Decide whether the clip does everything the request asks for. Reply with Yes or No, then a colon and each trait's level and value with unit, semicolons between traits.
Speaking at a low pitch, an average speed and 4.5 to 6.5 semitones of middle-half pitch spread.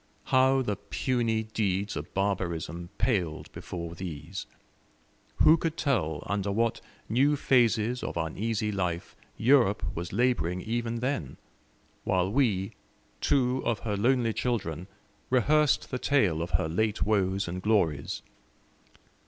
No: low, 105 Hz; slow, 125 wpm; wide, 5.6 semitones